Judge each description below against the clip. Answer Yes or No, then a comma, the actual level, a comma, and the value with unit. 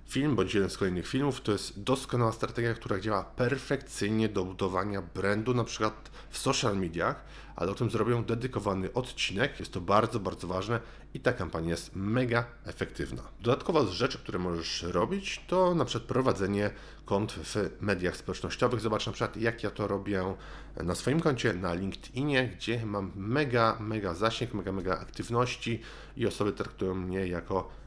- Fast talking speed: Yes, fast, 165 wpm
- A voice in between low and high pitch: No, low, 110 Hz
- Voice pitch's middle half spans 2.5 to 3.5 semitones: No, average, 4.5 semitones